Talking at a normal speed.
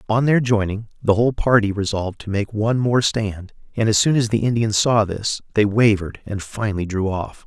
No: fast, 210 wpm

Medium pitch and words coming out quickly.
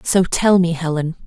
No: medium, 170 Hz; average, 190 wpm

